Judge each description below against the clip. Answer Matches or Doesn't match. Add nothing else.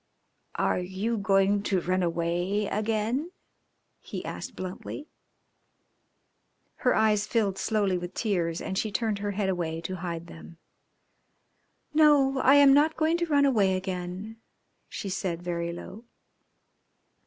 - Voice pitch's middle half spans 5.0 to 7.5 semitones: Doesn't match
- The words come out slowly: Matches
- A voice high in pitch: Matches